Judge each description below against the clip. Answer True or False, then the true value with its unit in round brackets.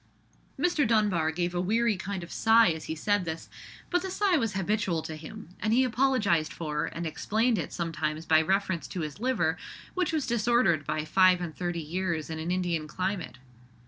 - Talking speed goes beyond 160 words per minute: True (190 wpm)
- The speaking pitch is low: False (180 Hz)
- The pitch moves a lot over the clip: True (5.7 semitones)